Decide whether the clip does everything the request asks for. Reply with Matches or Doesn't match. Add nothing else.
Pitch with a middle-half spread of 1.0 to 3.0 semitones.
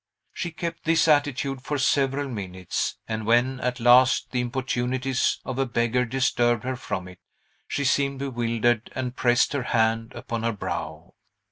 Matches